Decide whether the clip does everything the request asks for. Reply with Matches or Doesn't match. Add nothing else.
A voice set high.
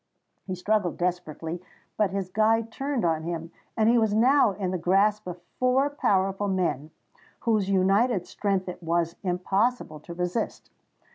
Matches